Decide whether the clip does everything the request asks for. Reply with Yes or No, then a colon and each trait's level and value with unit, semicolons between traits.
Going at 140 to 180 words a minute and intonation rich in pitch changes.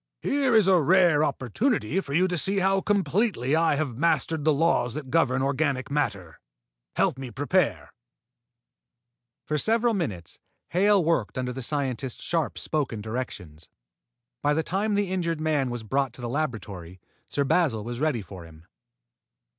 Yes: average, 155 wpm; wide, 6.3 semitones